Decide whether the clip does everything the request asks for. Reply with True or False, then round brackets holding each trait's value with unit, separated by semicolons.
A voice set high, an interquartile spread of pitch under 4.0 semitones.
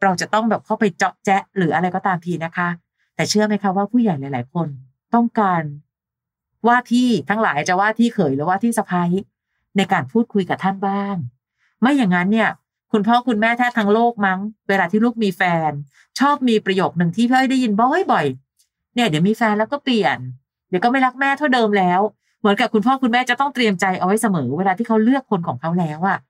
False (200 Hz; 4.7 semitones)